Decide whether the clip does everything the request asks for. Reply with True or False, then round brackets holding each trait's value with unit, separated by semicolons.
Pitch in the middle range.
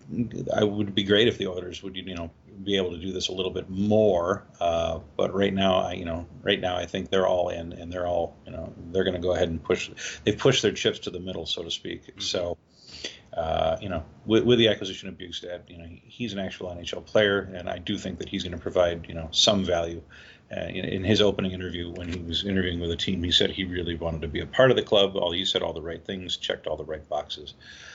False (90 Hz)